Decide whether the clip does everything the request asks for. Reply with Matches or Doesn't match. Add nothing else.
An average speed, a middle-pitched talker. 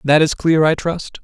Doesn't match